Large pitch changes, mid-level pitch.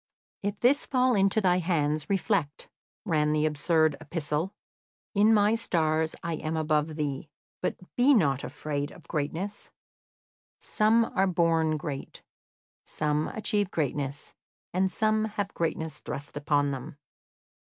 No: average, 5.0 semitones; medium, 160 Hz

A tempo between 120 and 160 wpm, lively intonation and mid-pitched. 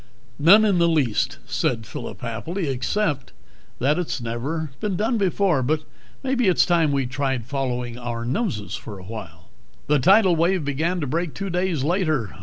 No: average, 170 wpm; wide, 6.4 semitones; medium, 150 Hz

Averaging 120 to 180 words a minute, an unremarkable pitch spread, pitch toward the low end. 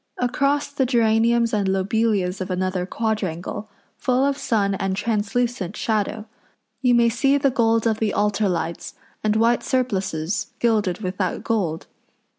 No: average, 145 wpm; average, 3.7 semitones; high, 220 Hz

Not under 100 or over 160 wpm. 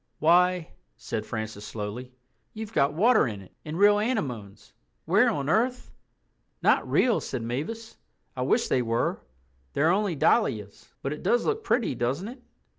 Yes: average, 150 wpm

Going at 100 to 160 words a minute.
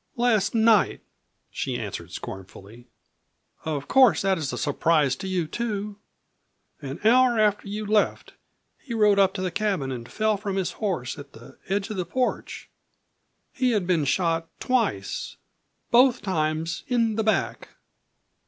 Yes: average, 150 wpm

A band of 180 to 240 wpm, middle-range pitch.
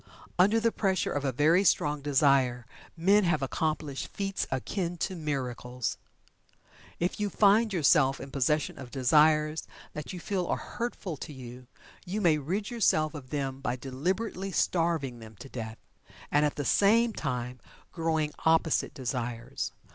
No: average, 150 wpm; medium, 150 Hz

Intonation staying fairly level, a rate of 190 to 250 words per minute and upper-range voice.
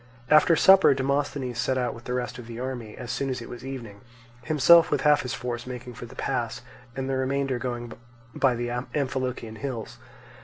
No: narrow, 2.2 semitones; average, 195 wpm; low, 125 Hz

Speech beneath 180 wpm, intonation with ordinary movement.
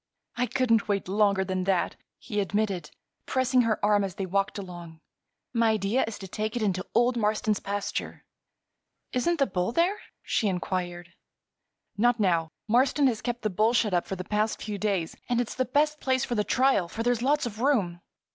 No: average, 185 wpm; average, 4.1 semitones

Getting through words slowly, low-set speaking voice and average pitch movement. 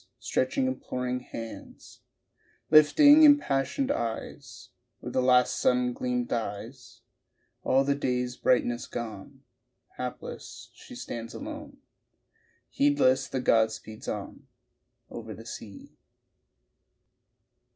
Yes: slow, 100 wpm; low, 125 Hz; average, 4.6 semitones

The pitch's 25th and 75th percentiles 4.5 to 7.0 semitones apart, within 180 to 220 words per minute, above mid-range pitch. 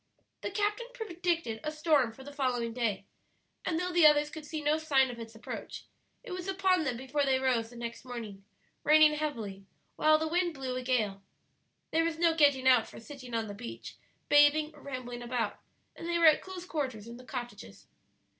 Yes: average, 4.9 semitones; average, 200 wpm; very high, 280 Hz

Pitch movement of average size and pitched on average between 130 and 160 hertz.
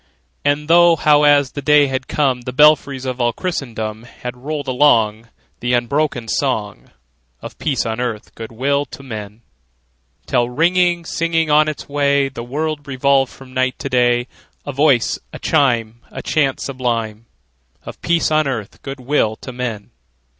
Yes: average, 3.4 semitones; low, 135 Hz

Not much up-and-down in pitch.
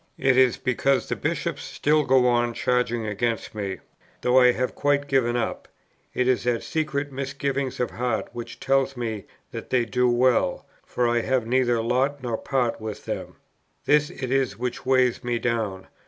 Yes: narrow, 2.3 semitones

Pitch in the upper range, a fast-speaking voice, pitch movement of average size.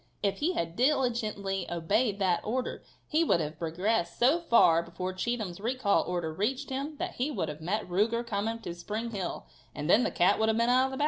No: high, 210 Hz; fast, 215 wpm; wide, 6.0 semitones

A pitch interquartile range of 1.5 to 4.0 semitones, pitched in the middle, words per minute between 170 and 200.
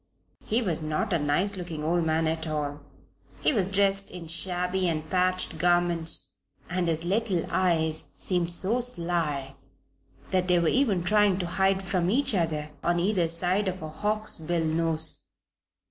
No: average, 3.0 semitones; medium, 175 Hz; average, 160 wpm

